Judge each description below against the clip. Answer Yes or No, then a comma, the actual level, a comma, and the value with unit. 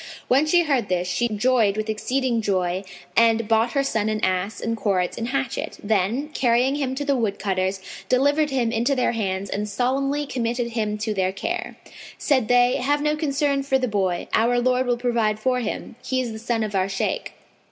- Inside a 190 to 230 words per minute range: Yes, average, 195 wpm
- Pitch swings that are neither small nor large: Yes, average, 3.9 semitones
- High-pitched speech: Yes, high, 235 Hz